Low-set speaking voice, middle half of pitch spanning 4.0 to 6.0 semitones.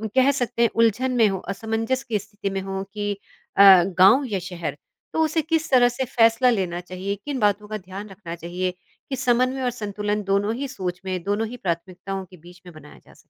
No: high, 205 Hz; average, 4.6 semitones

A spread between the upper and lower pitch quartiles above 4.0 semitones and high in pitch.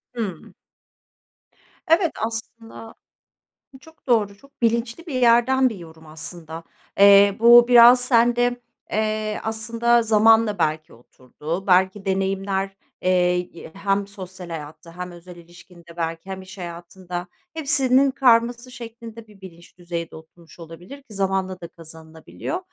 Yes: average, 5.2 semitones; high, 195 Hz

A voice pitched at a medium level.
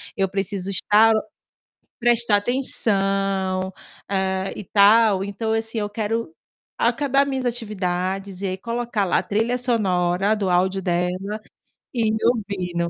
No: high, 205 Hz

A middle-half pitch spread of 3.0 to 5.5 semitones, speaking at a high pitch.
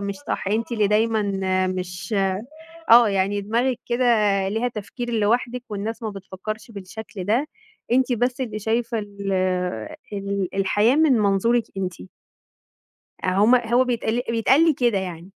Yes: average, 3.4 semitones; high, 220 Hz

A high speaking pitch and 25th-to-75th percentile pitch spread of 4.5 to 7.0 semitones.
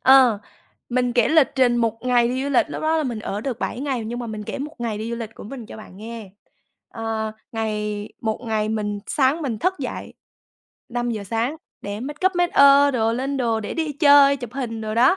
No: high, 240 Hz; average, 3.8 semitones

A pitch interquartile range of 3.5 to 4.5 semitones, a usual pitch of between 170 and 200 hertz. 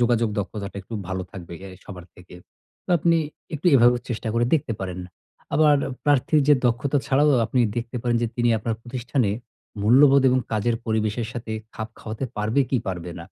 No: average, 3.8 semitones; low, 120 Hz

